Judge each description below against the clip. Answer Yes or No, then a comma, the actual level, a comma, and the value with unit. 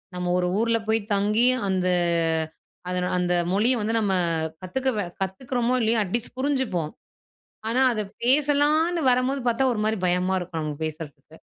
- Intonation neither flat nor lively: No, wide, 5.9 semitones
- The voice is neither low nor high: No, high, 215 Hz